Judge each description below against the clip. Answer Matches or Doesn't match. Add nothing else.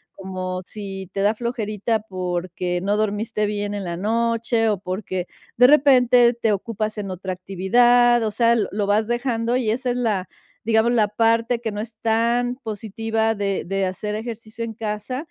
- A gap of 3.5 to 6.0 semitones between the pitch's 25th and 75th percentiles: Doesn't match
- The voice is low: Doesn't match